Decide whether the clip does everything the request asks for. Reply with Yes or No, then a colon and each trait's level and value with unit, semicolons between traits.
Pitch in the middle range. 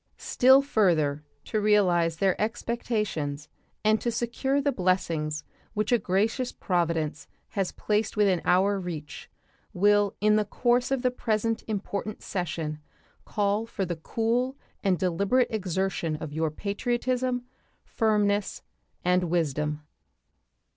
No: high, 200 Hz